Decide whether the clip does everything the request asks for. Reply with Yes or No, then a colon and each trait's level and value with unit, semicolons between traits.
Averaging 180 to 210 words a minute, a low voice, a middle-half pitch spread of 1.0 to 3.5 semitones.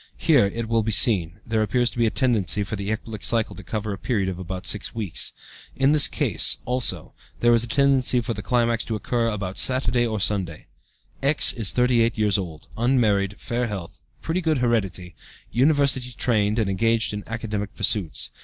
Yes: average, 190 wpm; low, 110 Hz; average, 3.2 semitones